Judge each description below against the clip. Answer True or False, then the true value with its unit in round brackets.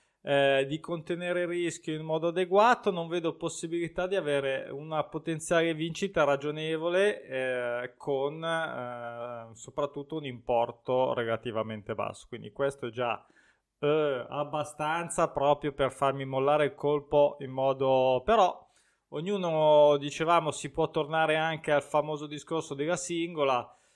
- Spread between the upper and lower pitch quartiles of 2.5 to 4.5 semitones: True (3.3 semitones)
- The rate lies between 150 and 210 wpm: False (130 wpm)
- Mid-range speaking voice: True (150 Hz)